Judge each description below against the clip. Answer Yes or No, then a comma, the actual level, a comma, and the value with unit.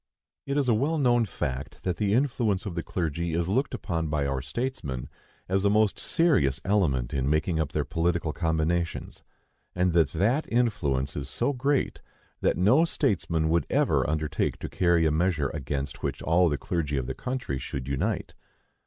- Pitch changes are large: Yes, wide, 6.7 semitones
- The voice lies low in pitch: Yes, very low, 85 Hz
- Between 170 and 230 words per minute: Yes, average, 180 wpm